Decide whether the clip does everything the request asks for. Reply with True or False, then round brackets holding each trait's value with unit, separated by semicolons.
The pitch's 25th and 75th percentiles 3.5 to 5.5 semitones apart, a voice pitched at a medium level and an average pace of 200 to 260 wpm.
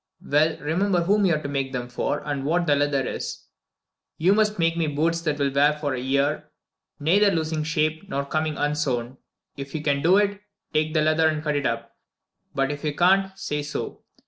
False (2.9 semitones; 150 Hz; 205 wpm)